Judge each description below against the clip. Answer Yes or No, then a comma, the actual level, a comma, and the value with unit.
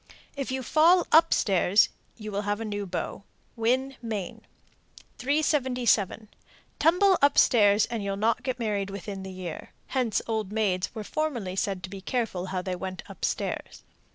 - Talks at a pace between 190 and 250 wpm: No, average, 165 wpm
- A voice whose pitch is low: No, high, 215 Hz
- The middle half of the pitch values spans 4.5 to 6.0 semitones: Yes, average, 4.8 semitones